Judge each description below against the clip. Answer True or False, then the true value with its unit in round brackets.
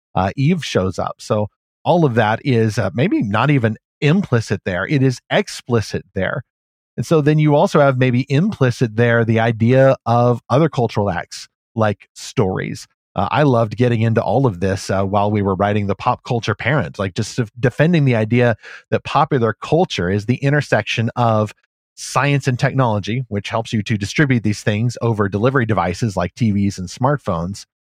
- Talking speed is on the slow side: False (175 wpm)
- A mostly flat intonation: False (4.1 semitones)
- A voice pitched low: True (120 Hz)